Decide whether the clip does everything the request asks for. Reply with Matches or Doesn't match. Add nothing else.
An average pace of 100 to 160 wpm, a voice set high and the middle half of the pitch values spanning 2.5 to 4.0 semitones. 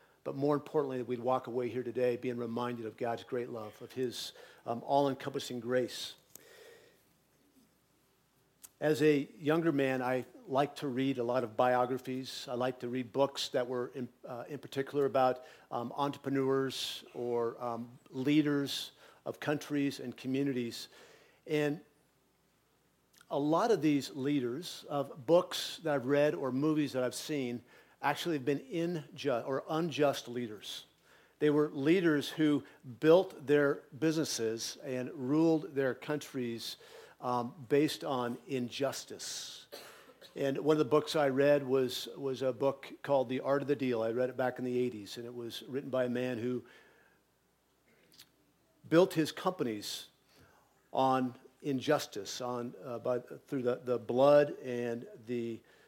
Doesn't match